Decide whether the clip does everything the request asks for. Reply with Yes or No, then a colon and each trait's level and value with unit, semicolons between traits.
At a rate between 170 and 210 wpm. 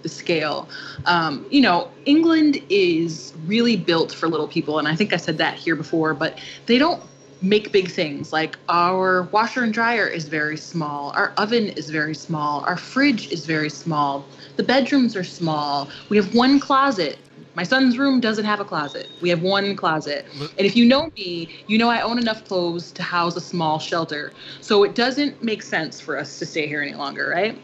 Yes: average, 200 wpm